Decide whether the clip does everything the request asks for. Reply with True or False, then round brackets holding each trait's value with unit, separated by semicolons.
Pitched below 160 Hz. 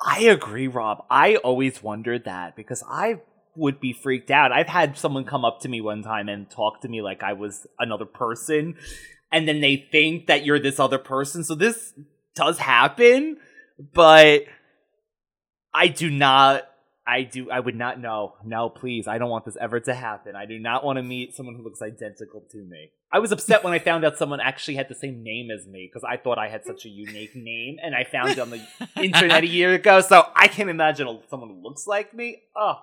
True (135 Hz)